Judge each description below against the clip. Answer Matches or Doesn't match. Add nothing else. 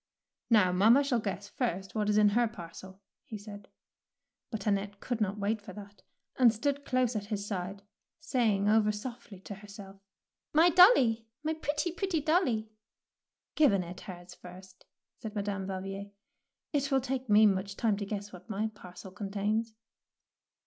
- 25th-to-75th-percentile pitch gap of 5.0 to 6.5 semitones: Doesn't match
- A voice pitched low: Doesn't match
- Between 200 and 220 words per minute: Doesn't match